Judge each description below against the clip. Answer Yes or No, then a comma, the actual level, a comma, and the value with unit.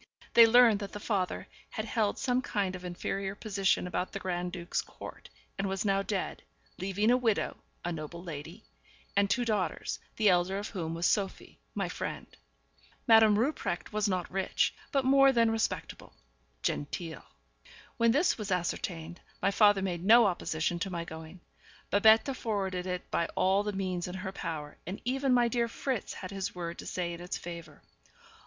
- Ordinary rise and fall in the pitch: Yes, average, 3.7 semitones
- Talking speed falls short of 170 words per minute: No, average, 175 wpm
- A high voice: Yes, high, 195 Hz